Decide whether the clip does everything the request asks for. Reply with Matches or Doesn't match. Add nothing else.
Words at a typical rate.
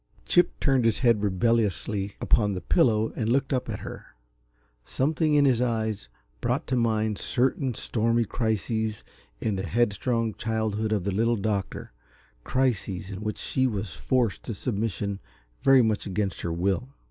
Matches